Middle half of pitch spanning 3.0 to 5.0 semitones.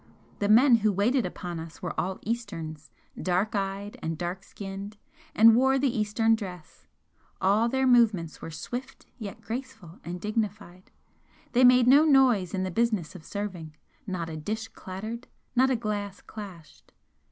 Yes: average, 4.3 semitones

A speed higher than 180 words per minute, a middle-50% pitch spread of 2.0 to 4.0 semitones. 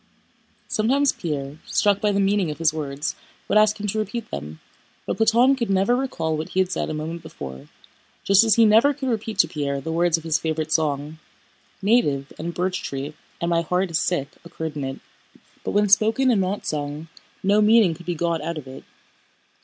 No: fast, 205 wpm; wide, 5.5 semitones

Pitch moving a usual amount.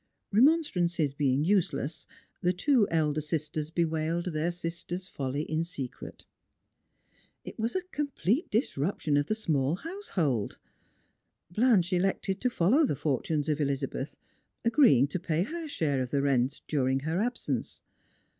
No: wide, 6.2 semitones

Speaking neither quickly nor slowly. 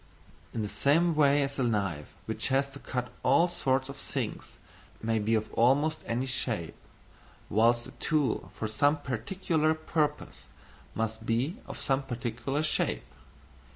Yes: average, 150 wpm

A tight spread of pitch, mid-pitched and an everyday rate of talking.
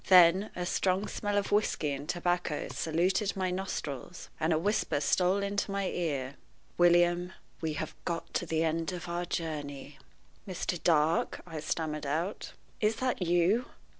No: average, 3.0 semitones; medium, 175 Hz; average, 155 wpm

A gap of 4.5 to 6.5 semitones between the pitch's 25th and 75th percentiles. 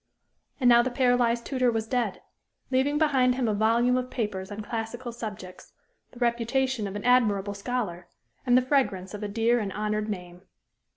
No: average, 3.2 semitones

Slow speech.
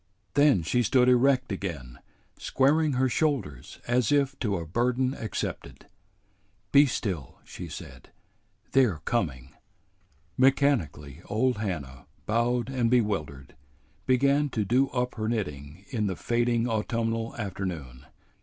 Yes: slow, 120 wpm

